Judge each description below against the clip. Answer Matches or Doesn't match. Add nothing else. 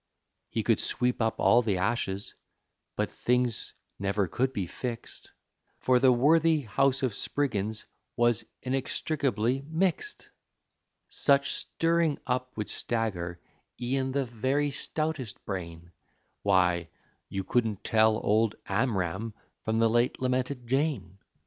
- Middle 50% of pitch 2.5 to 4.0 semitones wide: Doesn't match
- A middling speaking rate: Doesn't match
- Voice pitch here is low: Matches